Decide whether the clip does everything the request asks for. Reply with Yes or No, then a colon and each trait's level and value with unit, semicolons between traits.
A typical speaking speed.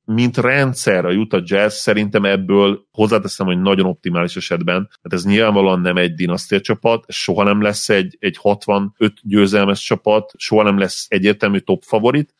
No: fast, 160 wpm